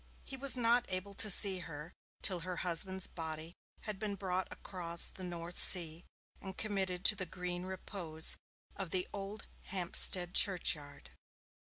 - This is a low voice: No, medium, 185 Hz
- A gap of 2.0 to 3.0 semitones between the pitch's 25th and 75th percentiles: Yes, narrow, 2.4 semitones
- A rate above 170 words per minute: No, average, 150 wpm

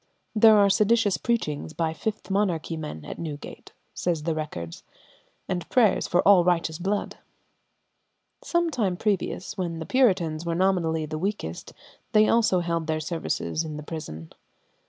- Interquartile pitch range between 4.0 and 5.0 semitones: Yes, average, 4.4 semitones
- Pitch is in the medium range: Yes, medium, 175 Hz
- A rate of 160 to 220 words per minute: No, average, 150 wpm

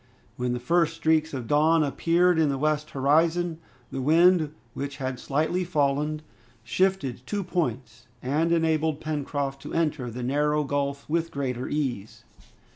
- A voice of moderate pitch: Yes, medium, 150 Hz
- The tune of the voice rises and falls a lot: No, average, 3.1 semitones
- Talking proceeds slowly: No, average, 145 wpm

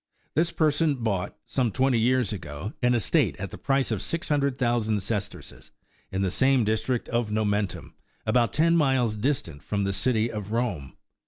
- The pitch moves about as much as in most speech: Yes, average, 4.3 semitones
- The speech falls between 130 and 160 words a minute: No, average, 170 wpm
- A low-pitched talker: Yes, low, 115 Hz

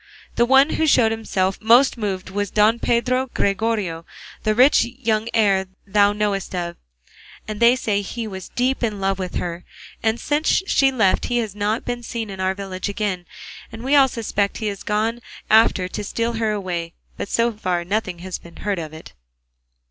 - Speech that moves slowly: No, average, 190 wpm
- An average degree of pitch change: Yes, average, 3.4 semitones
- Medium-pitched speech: No, high, 210 Hz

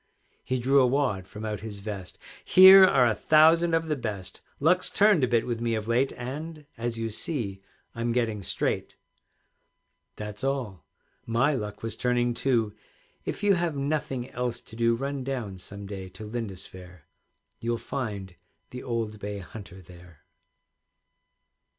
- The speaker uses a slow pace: No, average, 155 wpm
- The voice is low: Yes, low, 115 Hz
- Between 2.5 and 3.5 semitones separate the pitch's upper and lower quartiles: No, average, 4.8 semitones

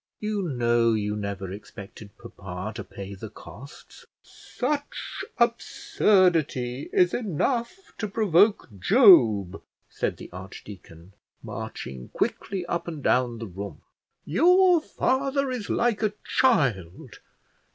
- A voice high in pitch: No, medium, 140 Hz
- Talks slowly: Yes, slow, 110 wpm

